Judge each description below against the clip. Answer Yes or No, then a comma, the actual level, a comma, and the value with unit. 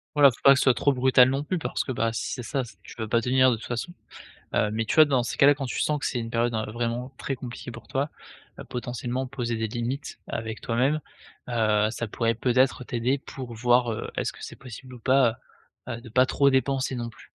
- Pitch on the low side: Yes, low, 125 Hz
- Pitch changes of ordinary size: No, narrow, 2.3 semitones